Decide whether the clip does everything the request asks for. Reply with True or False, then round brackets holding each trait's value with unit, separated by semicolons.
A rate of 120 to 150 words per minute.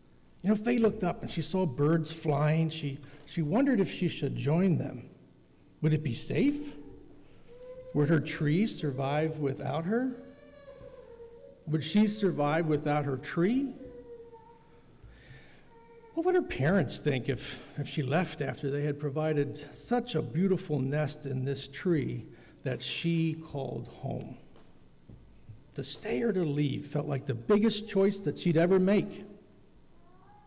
True (145 wpm)